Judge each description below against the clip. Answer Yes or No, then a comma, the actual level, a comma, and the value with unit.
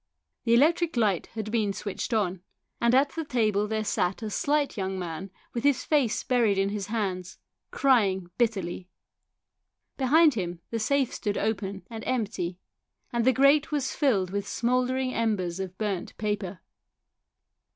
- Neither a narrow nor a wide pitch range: Yes, average, 4.7 semitones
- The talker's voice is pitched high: Yes, high, 215 Hz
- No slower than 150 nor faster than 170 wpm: Yes, average, 155 wpm